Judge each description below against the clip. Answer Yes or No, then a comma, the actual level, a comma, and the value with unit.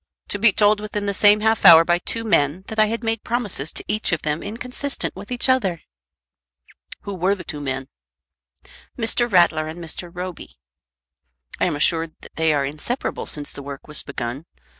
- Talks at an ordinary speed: Yes, average, 185 wpm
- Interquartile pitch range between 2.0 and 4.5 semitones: No, wide, 5.6 semitones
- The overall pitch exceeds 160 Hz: Yes, medium, 185 Hz